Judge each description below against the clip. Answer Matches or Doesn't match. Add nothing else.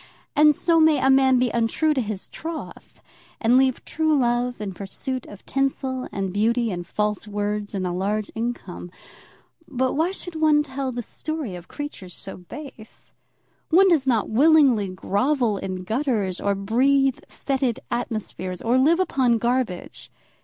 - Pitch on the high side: Matches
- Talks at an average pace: Matches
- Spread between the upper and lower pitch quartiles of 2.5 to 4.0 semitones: Doesn't match